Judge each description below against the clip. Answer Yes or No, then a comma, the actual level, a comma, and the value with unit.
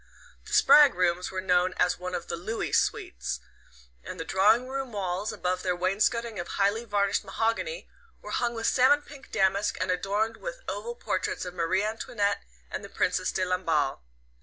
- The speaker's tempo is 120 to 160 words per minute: No, average, 175 wpm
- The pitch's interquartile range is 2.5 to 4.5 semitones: Yes, average, 3.9 semitones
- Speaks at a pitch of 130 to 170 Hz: No, high, 200 Hz